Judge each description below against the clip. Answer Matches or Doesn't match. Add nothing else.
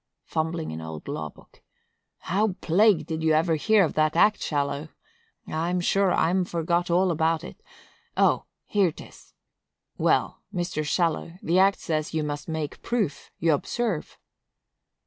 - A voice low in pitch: Doesn't match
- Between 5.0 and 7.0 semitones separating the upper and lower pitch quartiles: Doesn't match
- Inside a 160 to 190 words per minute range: Doesn't match